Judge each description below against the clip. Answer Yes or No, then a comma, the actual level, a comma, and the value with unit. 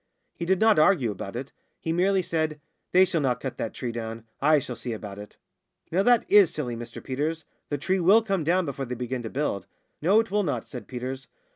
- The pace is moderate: No, fast, 225 wpm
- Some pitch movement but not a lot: No, wide, 7.0 semitones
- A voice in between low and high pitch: Yes, medium, 150 Hz